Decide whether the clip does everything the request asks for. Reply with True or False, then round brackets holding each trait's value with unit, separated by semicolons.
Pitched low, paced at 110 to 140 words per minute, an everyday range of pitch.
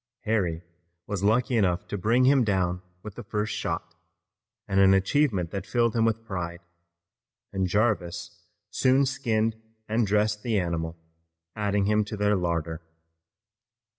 True (105 Hz; 135 wpm; 4.0 semitones)